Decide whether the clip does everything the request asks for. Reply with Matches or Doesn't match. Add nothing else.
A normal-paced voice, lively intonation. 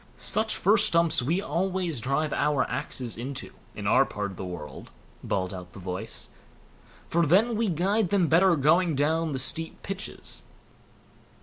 Matches